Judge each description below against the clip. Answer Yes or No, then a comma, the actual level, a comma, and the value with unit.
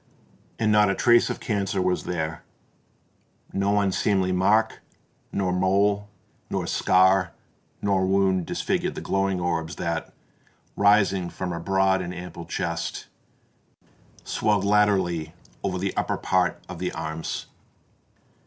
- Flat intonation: Yes, narrow, 2.1 semitones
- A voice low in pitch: Yes, very low, 95 Hz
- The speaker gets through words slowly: Yes, slow, 125 wpm